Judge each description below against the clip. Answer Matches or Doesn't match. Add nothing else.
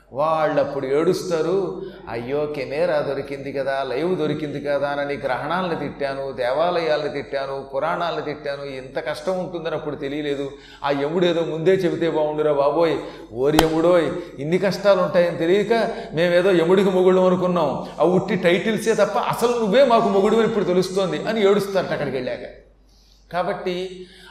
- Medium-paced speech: Doesn't match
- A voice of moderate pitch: Matches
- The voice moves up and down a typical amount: Matches